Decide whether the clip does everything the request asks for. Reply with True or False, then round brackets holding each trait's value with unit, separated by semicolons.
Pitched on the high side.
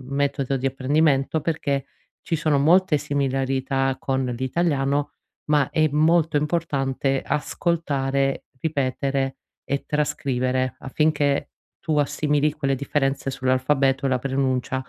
False (140 Hz)